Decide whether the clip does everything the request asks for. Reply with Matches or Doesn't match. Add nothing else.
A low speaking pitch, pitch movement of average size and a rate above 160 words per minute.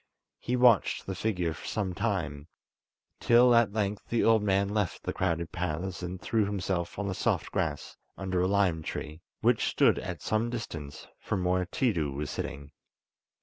Matches